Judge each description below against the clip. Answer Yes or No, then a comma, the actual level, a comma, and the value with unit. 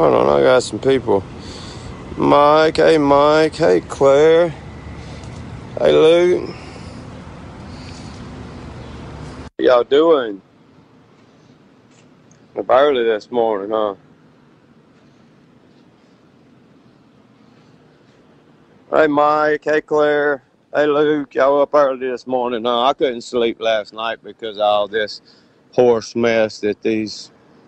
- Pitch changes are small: No, average, 5.1 semitones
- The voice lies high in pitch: No, low, 125 Hz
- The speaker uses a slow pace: Yes, slow, 100 wpm